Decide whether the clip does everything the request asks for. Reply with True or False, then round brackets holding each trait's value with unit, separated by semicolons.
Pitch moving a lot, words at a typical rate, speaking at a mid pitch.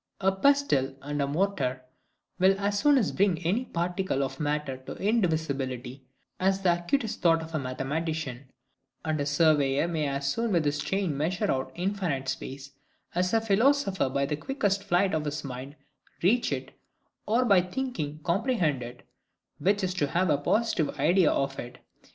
True (5.8 semitones; 160 wpm; 165 Hz)